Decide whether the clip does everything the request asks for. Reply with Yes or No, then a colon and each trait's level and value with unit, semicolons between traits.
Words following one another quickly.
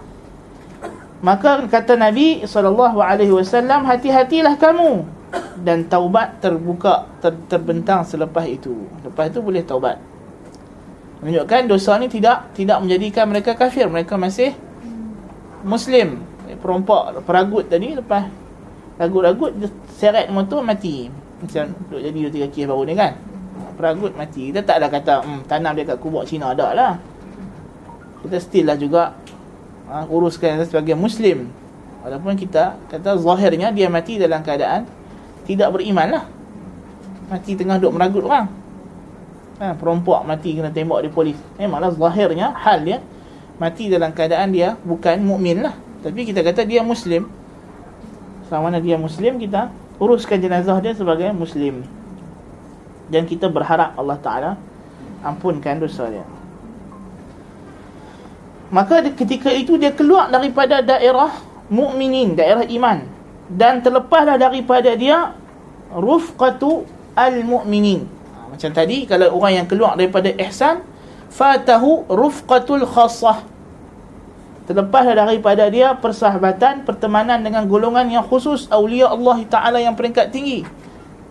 No: average, 120 wpm